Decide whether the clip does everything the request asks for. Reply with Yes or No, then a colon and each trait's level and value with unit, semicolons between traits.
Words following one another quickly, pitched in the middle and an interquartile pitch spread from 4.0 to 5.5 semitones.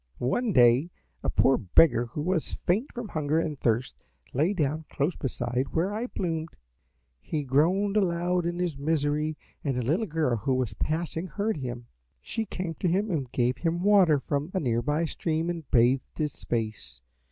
No: average, 175 wpm; medium, 155 Hz; average, 5.1 semitones